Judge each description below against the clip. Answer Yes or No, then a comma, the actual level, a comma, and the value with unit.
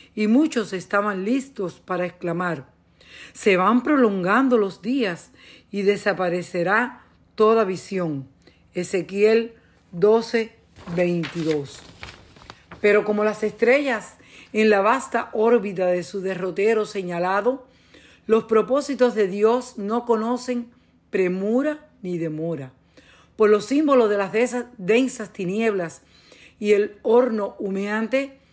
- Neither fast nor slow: No, slow, 105 wpm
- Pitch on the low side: No, high, 210 Hz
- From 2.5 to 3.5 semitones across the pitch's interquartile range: No, average, 4.1 semitones